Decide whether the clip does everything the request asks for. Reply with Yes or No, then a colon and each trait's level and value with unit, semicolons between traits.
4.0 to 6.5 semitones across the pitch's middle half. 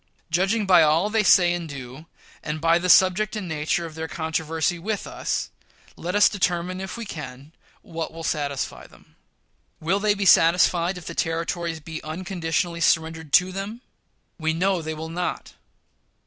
No: narrow, 2.6 semitones